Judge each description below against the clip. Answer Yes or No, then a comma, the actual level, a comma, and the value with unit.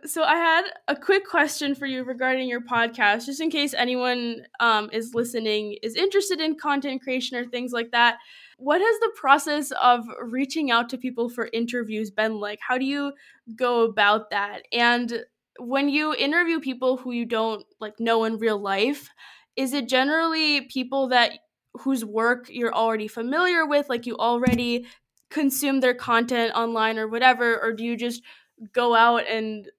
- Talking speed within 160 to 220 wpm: Yes, average, 175 wpm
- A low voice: No, high, 245 Hz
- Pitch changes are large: No, average, 3.4 semitones